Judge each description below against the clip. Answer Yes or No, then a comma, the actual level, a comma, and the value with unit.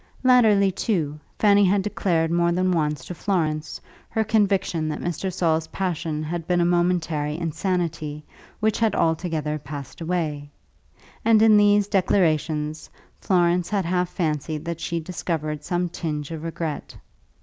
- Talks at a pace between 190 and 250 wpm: No, average, 140 wpm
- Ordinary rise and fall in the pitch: Yes, average, 3.3 semitones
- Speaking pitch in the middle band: Yes, medium, 170 Hz